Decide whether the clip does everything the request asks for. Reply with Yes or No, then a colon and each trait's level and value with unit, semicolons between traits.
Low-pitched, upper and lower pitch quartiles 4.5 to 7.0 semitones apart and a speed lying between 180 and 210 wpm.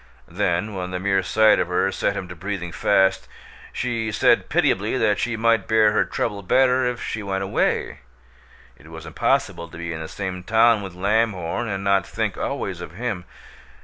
No: low, 100 Hz; average, 3.6 semitones; average, 185 wpm